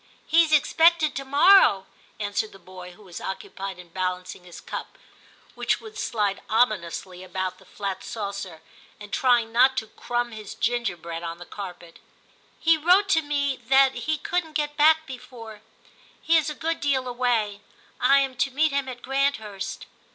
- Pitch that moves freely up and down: Yes, wide, 6.9 semitones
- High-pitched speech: Yes, high, 240 Hz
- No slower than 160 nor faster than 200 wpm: Yes, average, 175 wpm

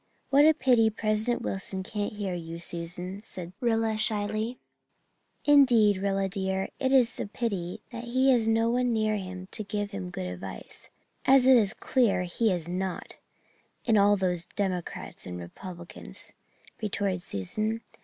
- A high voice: Yes, high, 205 Hz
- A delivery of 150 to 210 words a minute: Yes, average, 155 wpm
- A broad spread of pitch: No, average, 3.8 semitones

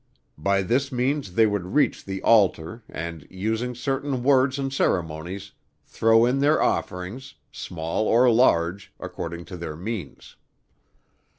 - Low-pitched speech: Yes, low, 110 Hz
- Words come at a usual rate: No, slow, 130 wpm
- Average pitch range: No, wide, 6.4 semitones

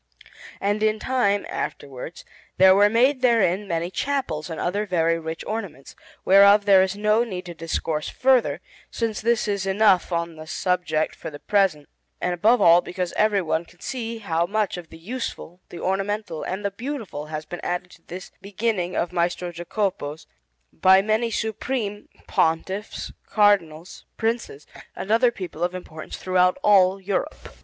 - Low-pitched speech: No, high, 190 Hz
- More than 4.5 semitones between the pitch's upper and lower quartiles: No, average, 3.8 semitones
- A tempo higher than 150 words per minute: Yes, average, 160 wpm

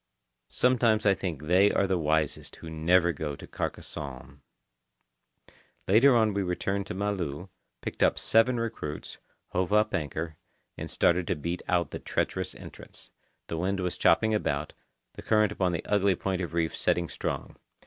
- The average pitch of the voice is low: Yes, very low, 90 Hz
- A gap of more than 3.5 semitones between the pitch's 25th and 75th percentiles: Yes, average, 4.2 semitones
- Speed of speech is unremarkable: Yes, average, 160 wpm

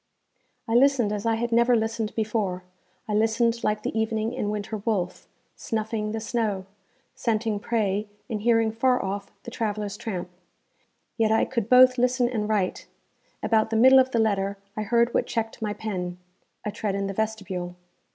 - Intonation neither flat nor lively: No, narrow, 2.1 semitones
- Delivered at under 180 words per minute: Yes, average, 170 wpm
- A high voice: Yes, high, 220 Hz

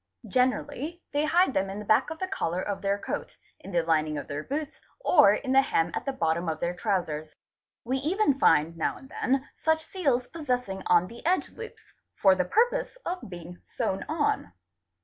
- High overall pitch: Yes, high, 235 Hz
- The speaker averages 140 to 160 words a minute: No, fast, 205 wpm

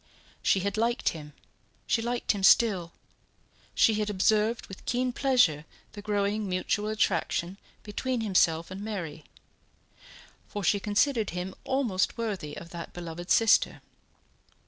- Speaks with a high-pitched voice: Yes, high, 205 Hz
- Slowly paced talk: Yes, slow, 130 wpm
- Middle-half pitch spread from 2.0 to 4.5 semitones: Yes, average, 4.0 semitones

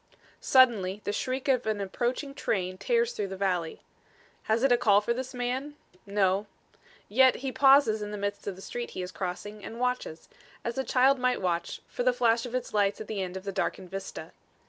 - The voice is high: Yes, high, 220 Hz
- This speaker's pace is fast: Yes, fast, 210 wpm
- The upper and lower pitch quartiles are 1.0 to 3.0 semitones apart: No, average, 4.5 semitones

